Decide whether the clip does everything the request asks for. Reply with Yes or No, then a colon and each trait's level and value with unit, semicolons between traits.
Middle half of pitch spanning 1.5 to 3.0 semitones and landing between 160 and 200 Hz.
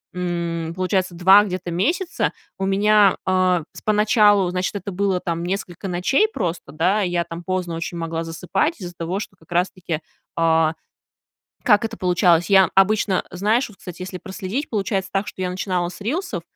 Yes: narrow, 2.6 semitones; medium, 185 Hz